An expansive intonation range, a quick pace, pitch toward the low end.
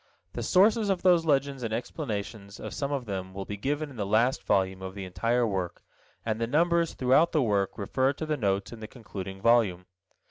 Yes: wide, 6.4 semitones; fast, 210 wpm; low, 115 Hz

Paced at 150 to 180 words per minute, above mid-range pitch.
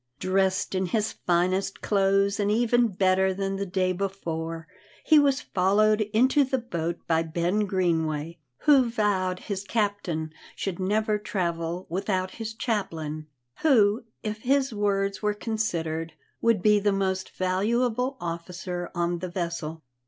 No: average, 140 wpm; high, 195 Hz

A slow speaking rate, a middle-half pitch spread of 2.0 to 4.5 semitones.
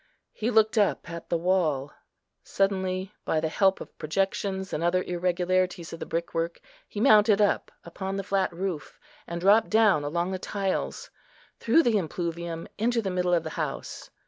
No: average, 170 wpm; average, 2.8 semitones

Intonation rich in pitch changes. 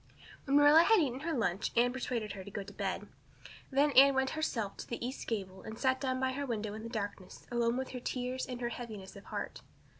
No: average, 3.6 semitones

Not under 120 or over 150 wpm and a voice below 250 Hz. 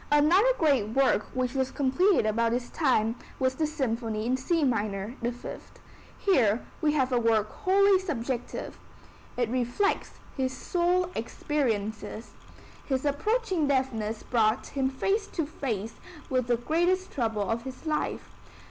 No: average, 140 wpm; very high, 260 Hz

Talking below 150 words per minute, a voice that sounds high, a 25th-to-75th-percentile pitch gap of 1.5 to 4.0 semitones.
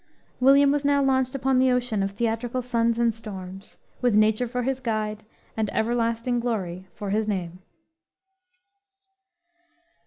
Yes: slow, 135 wpm; high, 230 Hz; average, 3.0 semitones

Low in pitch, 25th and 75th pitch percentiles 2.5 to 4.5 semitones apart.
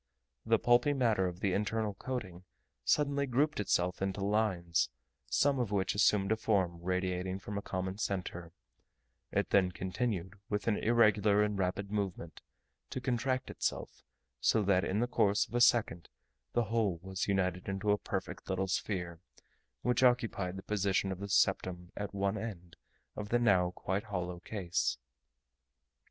Yes: low, 100 Hz; average, 3.1 semitones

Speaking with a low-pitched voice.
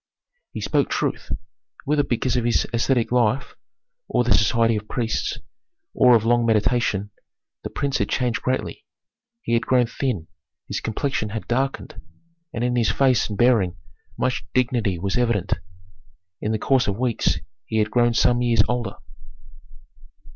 Yes: low, 120 Hz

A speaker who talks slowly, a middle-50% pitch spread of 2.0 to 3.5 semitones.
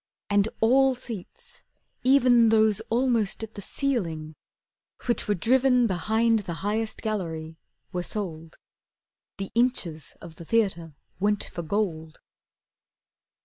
No: slow, 115 wpm; average, 5.3 semitones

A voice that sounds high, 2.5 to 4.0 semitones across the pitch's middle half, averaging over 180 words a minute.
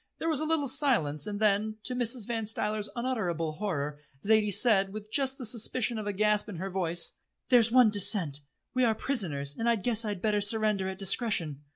Yes: high, 210 Hz; average, 3.7 semitones; average, 200 wpm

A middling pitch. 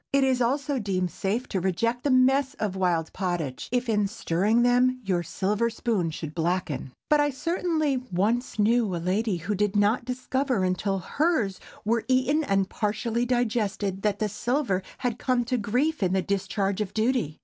No: high, 215 Hz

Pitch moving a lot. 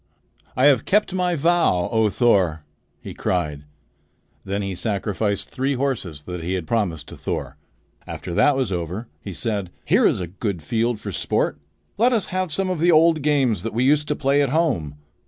Yes: wide, 8.2 semitones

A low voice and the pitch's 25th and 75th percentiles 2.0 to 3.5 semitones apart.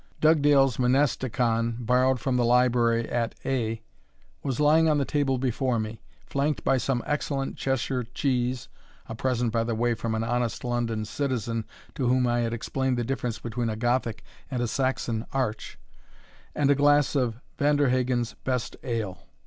Yes: low, 125 Hz; narrow, 2.6 semitones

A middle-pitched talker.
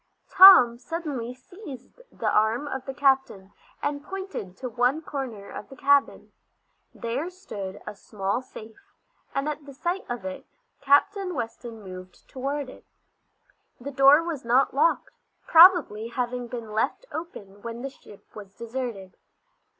No: very high, 255 Hz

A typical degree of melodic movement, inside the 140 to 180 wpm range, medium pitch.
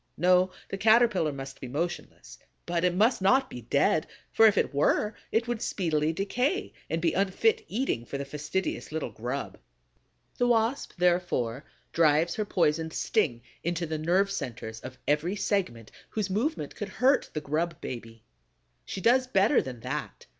No: wide, 6.7 semitones; average, 160 wpm; medium, 175 Hz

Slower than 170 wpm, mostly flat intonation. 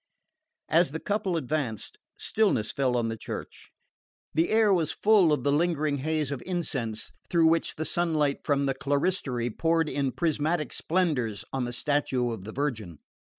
No: average, 160 wpm; average, 4.9 semitones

